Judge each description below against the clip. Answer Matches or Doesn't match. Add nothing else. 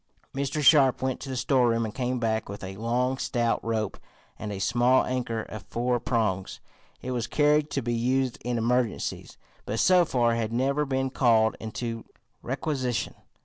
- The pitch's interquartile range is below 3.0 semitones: Matches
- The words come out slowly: Doesn't match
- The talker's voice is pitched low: Matches